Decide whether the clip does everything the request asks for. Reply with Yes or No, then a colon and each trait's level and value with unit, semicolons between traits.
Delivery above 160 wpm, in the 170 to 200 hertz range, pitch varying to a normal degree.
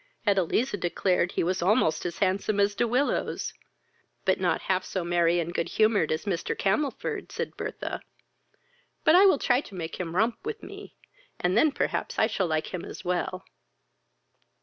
Yes: average, 170 wpm; high, 190 Hz; average, 4.2 semitones